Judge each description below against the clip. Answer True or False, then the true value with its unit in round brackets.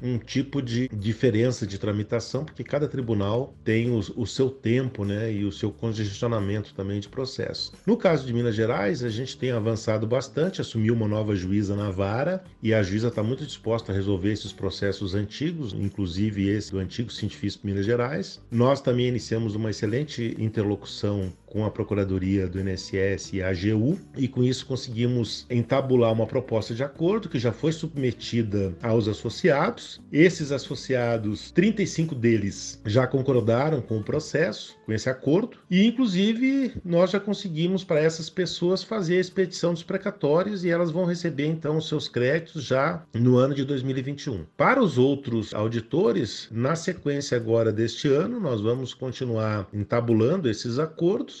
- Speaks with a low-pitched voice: True (120 Hz)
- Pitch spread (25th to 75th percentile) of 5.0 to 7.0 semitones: True (5.5 semitones)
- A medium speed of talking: True (160 wpm)